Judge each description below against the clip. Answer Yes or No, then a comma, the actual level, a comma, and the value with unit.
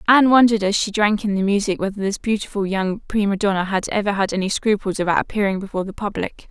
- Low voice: No, high, 200 Hz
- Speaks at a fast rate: Yes, fast, 220 wpm